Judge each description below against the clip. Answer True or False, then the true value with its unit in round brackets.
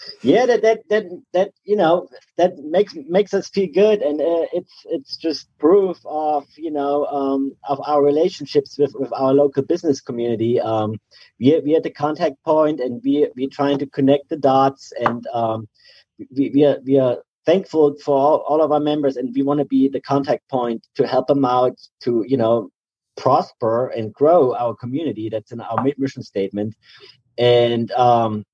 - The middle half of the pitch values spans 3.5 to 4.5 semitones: True (3.8 semitones)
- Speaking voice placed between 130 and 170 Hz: True (140 Hz)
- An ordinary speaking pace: True (190 wpm)